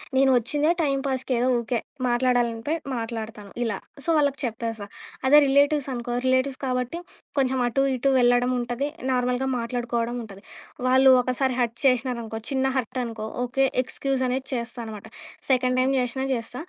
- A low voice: No, very high, 250 Hz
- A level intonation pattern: Yes, narrow, 2.1 semitones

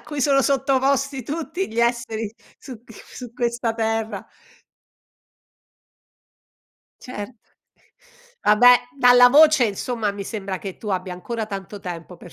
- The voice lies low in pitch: No, high, 235 Hz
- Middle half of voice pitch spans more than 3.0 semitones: Yes, average, 4.1 semitones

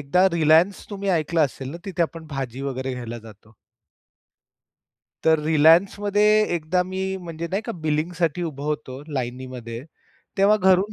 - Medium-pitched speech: Yes, medium, 160 Hz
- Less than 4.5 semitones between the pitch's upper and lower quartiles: No, wide, 5.4 semitones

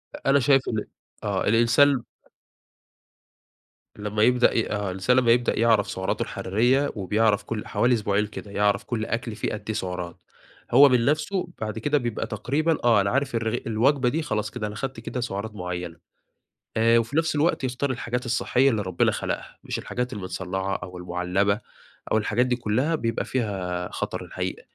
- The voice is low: Yes, low, 115 Hz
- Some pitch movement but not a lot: Yes, average, 3.6 semitones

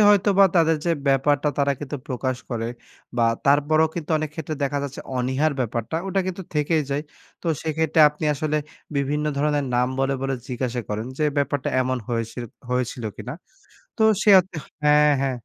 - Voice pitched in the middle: Yes, medium, 145 Hz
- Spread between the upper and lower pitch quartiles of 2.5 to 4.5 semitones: Yes, average, 3.2 semitones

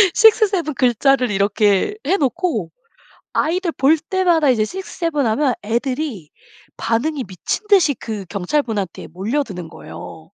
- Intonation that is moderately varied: No, wide, 7.6 semitones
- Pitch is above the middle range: Yes, very high, 275 Hz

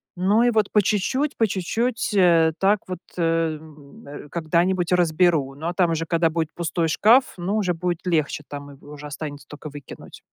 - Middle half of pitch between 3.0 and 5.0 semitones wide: Yes, average, 3.5 semitones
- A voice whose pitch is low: No, medium, 170 Hz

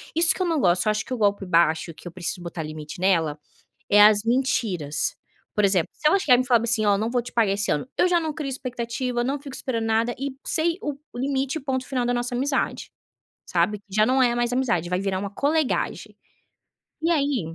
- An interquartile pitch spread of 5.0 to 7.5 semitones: Yes, wide, 5.4 semitones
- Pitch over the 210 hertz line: Yes, high, 240 Hz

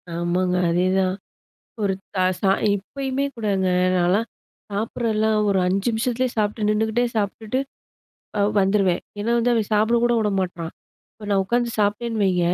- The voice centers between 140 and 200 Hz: No, high, 210 Hz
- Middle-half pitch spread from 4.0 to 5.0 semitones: No, average, 3.3 semitones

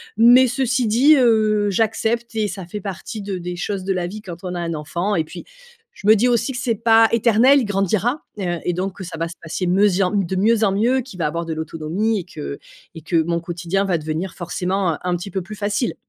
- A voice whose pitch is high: Yes, high, 195 Hz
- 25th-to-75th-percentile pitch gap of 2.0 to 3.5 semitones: No, average, 4.2 semitones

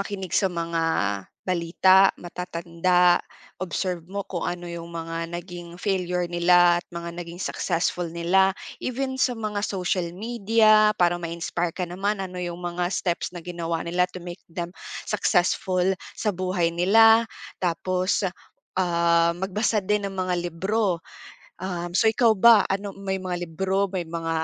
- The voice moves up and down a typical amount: No, narrow, 2.1 semitones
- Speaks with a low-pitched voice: No, medium, 180 Hz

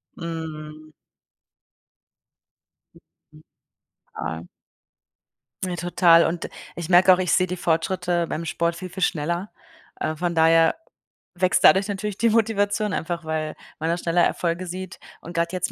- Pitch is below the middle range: No, medium, 175 Hz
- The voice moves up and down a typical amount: No, narrow, 2.2 semitones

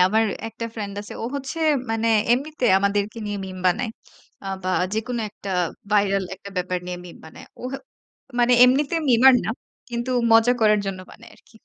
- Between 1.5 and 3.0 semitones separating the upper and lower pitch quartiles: No, average, 3.6 semitones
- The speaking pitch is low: No, high, 220 Hz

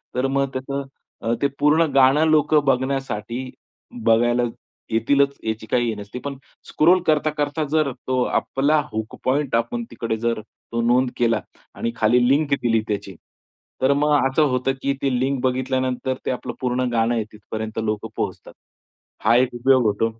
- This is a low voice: Yes, low, 130 Hz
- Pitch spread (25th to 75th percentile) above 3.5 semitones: No, average, 3.2 semitones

